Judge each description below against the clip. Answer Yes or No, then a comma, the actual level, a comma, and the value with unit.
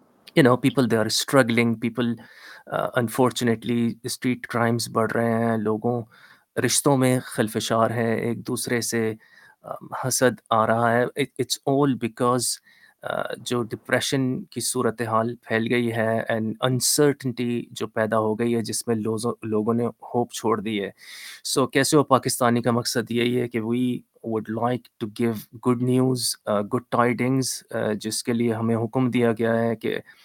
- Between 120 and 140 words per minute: No, average, 160 wpm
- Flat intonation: Yes, narrow, 1.7 semitones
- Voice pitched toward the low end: Yes, low, 120 Hz